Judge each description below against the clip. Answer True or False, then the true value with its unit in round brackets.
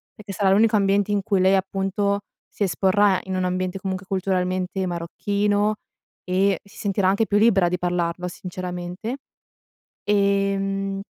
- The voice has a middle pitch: False (195 Hz)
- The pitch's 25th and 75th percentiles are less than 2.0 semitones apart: True (1.6 semitones)